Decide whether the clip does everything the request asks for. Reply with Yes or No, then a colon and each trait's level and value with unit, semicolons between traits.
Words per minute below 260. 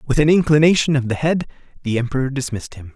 Yes: fast, 205 wpm